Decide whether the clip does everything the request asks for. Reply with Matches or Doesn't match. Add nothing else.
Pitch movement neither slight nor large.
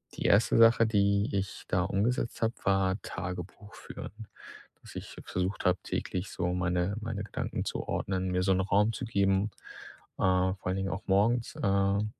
Doesn't match